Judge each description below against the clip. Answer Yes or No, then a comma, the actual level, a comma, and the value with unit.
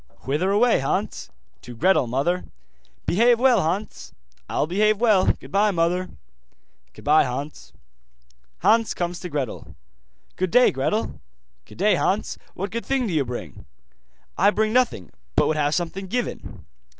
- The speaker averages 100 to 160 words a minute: Yes, average, 140 wpm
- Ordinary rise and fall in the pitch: No, wide, 6.2 semitones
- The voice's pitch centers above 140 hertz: Yes, medium, 185 Hz